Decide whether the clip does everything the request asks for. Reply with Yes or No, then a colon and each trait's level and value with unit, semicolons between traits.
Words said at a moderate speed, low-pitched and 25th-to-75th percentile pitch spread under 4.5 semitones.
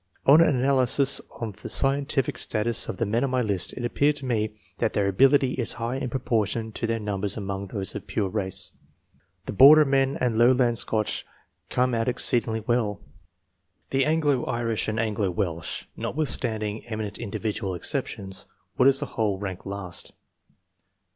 Yes: average, 165 wpm; low, 115 Hz; average, 4.1 semitones